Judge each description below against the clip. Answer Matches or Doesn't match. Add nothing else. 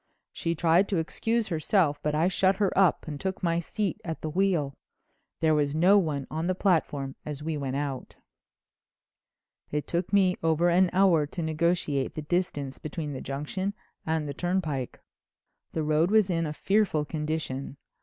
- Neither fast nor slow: Matches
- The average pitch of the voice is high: Doesn't match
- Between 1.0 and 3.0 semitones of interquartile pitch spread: Doesn't match